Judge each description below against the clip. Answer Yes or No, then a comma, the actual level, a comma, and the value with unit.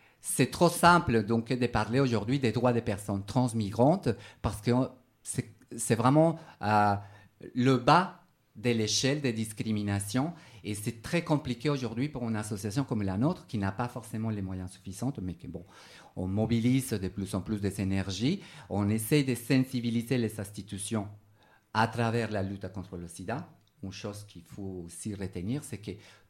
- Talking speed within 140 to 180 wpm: Yes, average, 165 wpm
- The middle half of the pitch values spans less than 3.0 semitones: No, average, 3.9 semitones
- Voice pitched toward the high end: No, low, 115 Hz